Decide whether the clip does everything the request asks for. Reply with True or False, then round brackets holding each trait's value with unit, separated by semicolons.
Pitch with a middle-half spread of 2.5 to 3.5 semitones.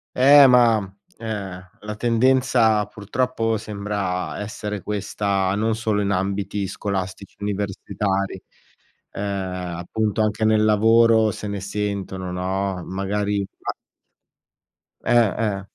False (2.1 semitones)